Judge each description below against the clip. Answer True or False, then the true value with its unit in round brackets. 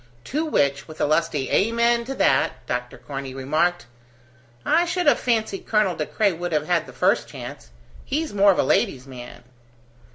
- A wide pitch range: True (8.9 semitones)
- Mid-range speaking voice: True (175 Hz)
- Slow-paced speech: False (175 wpm)